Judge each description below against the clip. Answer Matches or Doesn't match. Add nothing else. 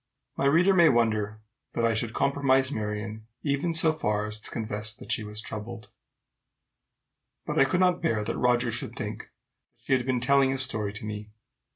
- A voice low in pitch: Matches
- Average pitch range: Matches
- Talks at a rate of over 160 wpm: Matches